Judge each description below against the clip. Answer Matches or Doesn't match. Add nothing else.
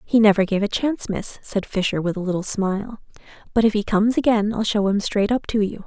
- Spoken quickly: Matches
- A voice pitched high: Matches